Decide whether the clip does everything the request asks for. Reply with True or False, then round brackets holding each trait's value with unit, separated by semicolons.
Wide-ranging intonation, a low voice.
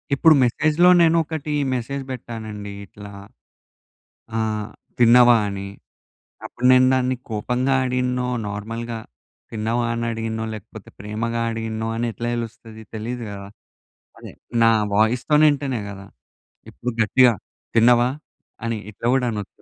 False (2.5 semitones; 115 Hz)